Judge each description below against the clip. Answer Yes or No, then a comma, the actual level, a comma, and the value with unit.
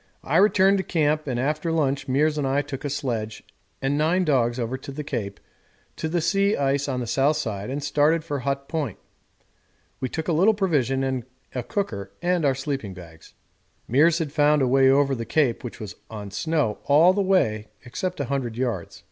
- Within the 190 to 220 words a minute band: Yes, average, 200 wpm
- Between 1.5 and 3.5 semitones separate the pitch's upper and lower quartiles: No, average, 4.1 semitones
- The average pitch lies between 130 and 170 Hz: Yes, medium, 140 Hz